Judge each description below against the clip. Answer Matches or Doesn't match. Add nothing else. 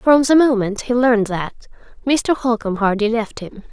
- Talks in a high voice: Matches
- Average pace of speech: Matches